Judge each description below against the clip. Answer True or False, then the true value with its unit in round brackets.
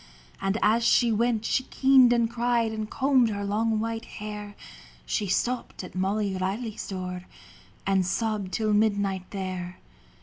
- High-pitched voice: True (215 Hz)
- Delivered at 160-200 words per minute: False (145 wpm)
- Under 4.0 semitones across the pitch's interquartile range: True (3.0 semitones)